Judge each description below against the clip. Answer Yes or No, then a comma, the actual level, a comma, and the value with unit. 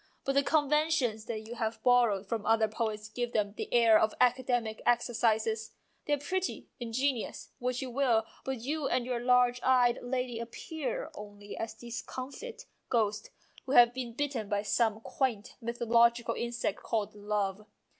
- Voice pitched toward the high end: Yes, high, 235 Hz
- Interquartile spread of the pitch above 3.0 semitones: No, average, 2.7 semitones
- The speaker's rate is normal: Yes, average, 160 wpm